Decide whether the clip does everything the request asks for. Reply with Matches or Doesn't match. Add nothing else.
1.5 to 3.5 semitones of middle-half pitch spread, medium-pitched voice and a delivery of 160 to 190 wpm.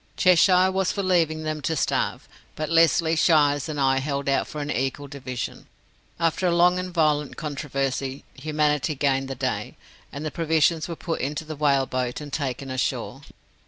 Matches